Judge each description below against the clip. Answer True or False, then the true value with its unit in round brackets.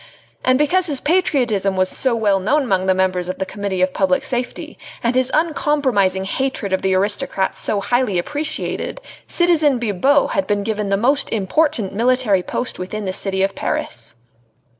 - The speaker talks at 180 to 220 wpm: False (170 wpm)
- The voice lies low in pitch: False (215 Hz)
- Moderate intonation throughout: False (6.1 semitones)